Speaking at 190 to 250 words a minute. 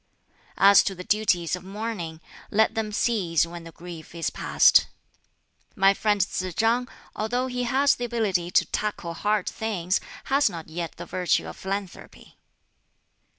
No: average, 150 wpm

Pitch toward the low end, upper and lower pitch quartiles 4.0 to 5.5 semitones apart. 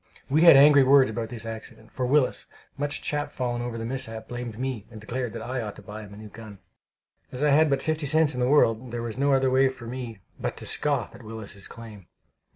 No: low, 125 Hz; average, 3.4 semitones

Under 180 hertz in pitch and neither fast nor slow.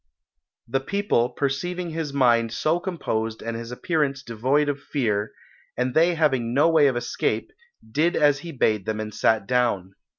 Yes: low, 135 Hz; average, 165 wpm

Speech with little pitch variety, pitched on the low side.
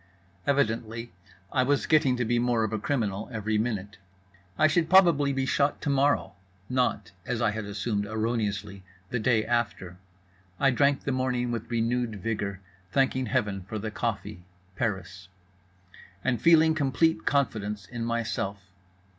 No: average, 3.9 semitones; low, 115 Hz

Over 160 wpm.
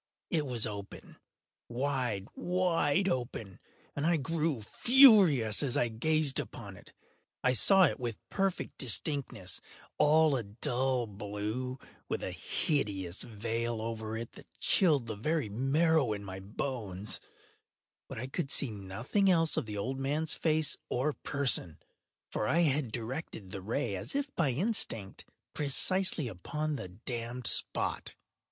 No: slow, 135 wpm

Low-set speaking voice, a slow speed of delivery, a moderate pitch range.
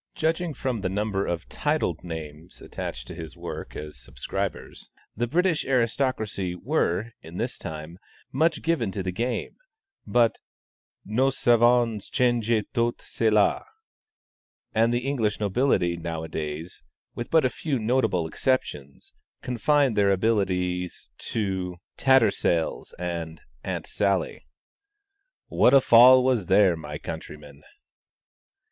No: low, 105 Hz; slow, 120 wpm; wide, 6.2 semitones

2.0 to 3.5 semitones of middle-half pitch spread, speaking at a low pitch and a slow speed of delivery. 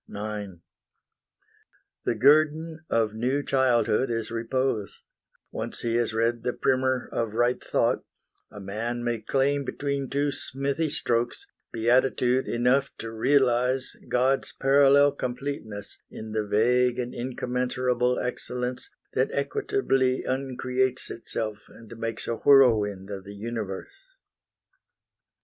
Yes: average, 2.9 semitones; low, 125 Hz; slow, 115 wpm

